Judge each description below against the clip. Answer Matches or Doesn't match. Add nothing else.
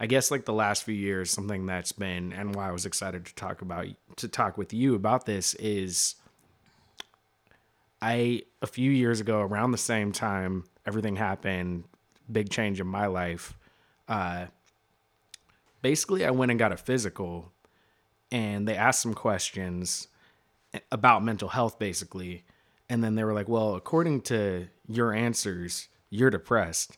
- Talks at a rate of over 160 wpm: Doesn't match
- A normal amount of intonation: Matches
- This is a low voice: Matches